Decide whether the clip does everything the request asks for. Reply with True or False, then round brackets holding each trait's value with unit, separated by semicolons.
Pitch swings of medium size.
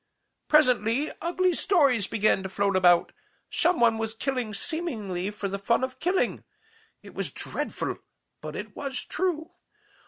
False (7.5 semitones)